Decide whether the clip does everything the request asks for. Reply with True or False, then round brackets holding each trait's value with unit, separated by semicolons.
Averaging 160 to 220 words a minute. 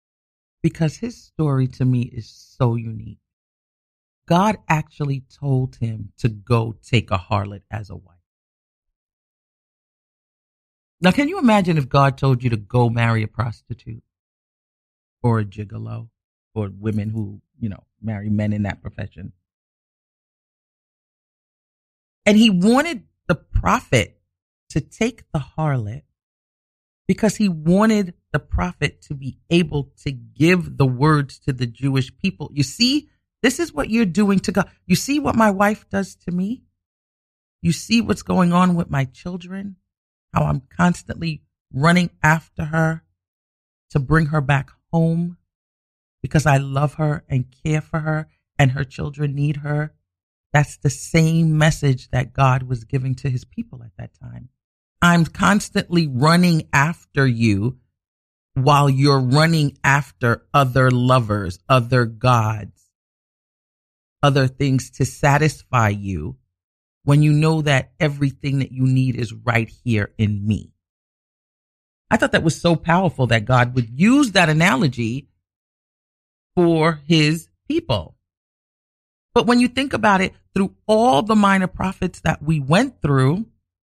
False (140 wpm)